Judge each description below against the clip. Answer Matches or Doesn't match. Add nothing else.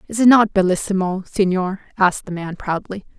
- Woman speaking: Matches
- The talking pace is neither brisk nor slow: Matches